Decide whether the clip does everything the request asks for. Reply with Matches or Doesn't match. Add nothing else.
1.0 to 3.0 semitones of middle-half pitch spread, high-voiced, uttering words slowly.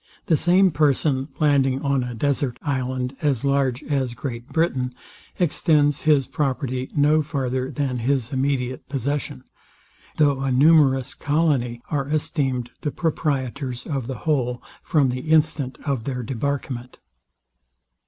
Doesn't match